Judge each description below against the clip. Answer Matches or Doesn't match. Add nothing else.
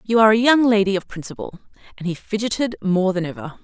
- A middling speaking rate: Doesn't match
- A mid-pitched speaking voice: Doesn't match